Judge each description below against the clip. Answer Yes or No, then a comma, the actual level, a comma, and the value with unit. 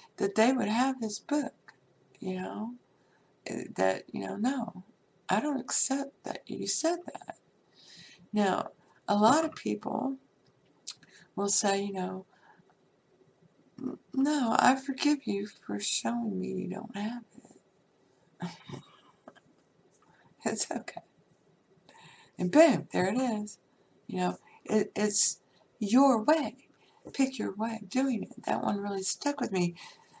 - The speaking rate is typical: No, slow, 125 wpm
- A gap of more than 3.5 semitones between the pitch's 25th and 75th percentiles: Yes, average, 5.2 semitones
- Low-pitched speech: No, high, 225 Hz